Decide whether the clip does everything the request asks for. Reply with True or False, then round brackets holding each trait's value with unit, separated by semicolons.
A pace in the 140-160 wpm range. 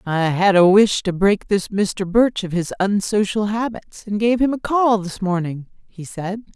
False (200 wpm)